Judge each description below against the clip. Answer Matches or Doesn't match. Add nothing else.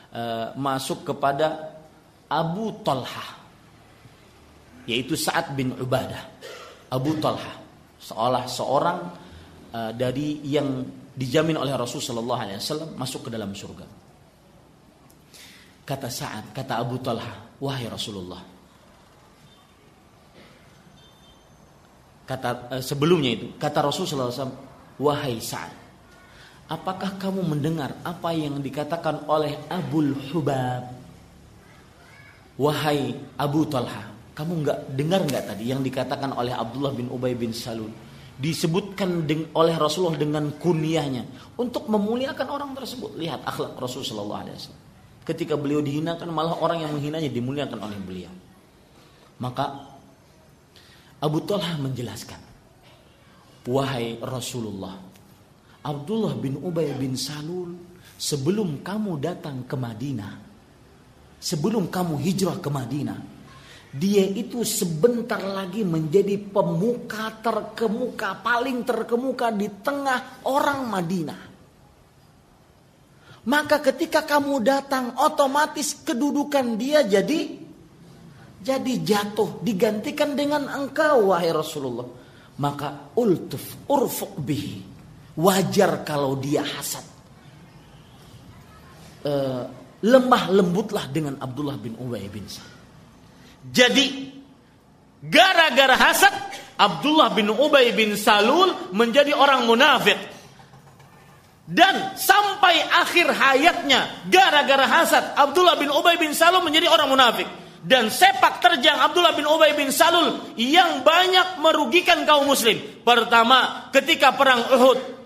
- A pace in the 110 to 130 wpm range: Doesn't match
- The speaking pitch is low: Doesn't match